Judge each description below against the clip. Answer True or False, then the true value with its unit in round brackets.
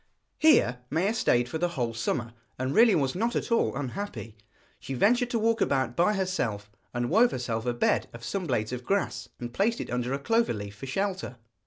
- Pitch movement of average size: False (8.9 semitones)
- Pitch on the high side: False (135 Hz)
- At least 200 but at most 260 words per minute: True (205 wpm)